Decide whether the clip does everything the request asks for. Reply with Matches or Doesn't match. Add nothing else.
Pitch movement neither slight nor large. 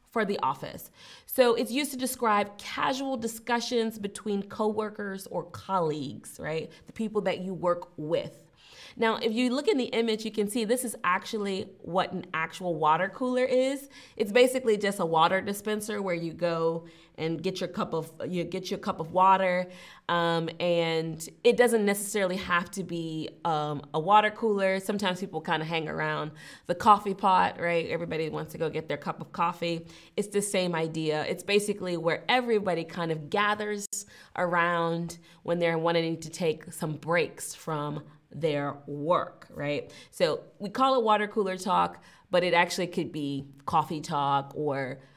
Matches